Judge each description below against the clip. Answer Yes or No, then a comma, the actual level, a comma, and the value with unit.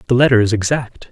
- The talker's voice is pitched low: Yes, low, 120 Hz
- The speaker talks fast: Yes, fast, 215 wpm